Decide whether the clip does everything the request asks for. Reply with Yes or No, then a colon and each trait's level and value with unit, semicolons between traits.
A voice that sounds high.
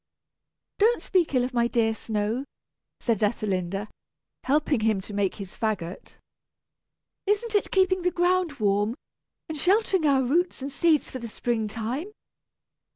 Yes: very high, 250 Hz